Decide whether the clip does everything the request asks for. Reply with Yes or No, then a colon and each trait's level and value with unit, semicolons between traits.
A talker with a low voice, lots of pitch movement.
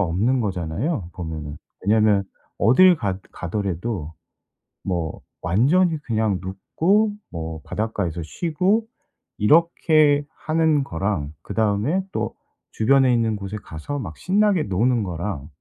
Yes: low, 105 Hz; wide, 8.6 semitones